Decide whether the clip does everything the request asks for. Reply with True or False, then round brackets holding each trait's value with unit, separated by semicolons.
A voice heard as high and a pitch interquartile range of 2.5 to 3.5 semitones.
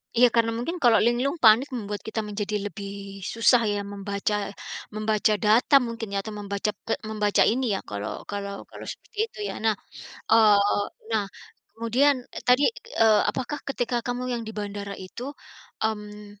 True (220 Hz; 2.8 semitones)